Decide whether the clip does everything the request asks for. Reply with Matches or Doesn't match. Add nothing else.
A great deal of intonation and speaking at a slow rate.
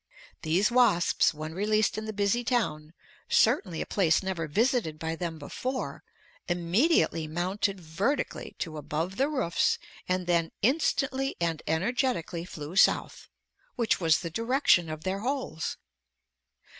Matches